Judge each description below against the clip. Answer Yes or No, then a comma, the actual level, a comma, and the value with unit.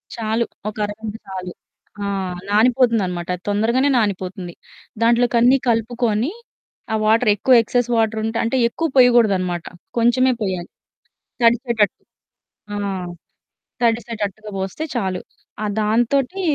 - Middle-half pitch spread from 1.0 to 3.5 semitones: Yes, average, 2.8 semitones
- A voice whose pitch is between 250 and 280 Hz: No, high, 225 Hz